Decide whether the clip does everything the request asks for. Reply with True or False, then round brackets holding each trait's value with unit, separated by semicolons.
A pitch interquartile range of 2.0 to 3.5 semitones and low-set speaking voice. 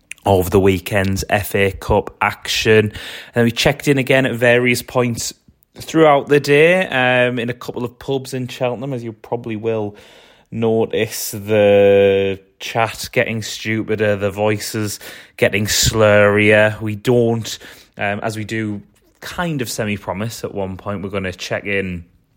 True (3.2 semitones; 110 Hz)